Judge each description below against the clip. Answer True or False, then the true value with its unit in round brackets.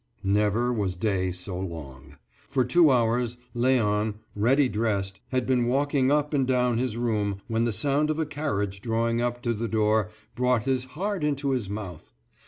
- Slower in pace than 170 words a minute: False (175 wpm)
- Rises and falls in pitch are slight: False (4.0 semitones)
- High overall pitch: False (120 Hz)